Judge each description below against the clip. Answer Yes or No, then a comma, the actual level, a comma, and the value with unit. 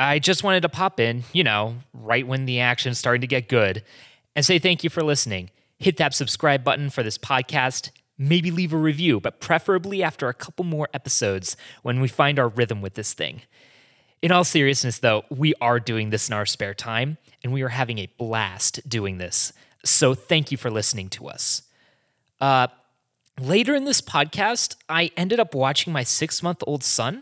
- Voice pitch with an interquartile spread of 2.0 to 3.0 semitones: No, average, 5.2 semitones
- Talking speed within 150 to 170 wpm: No, average, 200 wpm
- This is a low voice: Yes, low, 130 Hz